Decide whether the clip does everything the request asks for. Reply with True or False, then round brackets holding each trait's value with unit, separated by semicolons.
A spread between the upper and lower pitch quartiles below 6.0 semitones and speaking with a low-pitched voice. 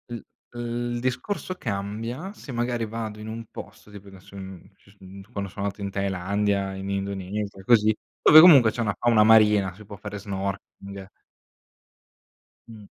True (2.6 semitones; 105 Hz)